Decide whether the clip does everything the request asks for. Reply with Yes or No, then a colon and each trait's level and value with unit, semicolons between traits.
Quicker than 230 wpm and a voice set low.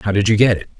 Yes: fast, 375 wpm; low, 105 Hz